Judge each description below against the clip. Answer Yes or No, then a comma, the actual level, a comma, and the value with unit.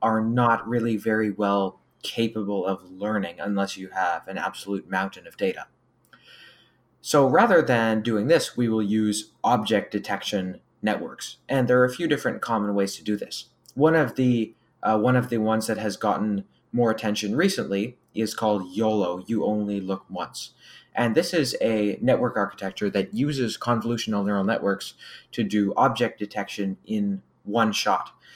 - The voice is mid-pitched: No, low, 110 Hz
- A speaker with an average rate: Yes, average, 165 wpm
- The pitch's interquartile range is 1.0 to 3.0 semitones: Yes, narrow, 2.6 semitones